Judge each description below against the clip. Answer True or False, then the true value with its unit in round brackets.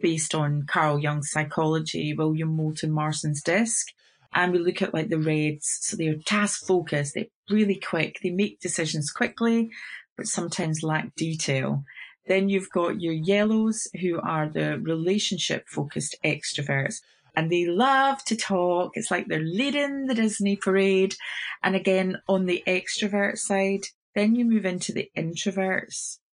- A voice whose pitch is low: False (180 Hz)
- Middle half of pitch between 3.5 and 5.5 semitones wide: True (4.1 semitones)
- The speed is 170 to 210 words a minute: False (155 wpm)